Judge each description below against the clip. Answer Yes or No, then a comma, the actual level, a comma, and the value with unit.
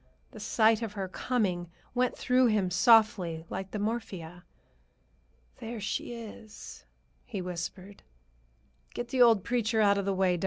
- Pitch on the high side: Yes, high, 210 Hz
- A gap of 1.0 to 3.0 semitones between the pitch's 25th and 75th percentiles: No, average, 3.7 semitones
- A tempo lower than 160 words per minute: Yes, average, 150 wpm